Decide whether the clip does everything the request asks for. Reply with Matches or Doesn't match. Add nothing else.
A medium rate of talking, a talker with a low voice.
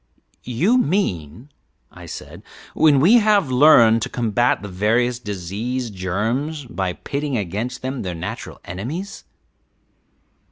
Doesn't match